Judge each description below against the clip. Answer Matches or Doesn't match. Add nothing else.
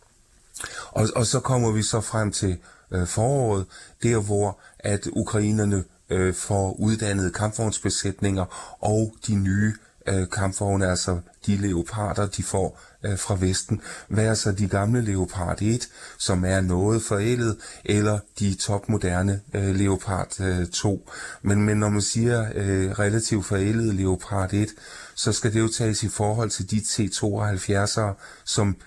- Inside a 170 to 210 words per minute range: Doesn't match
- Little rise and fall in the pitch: Matches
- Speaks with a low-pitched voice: Matches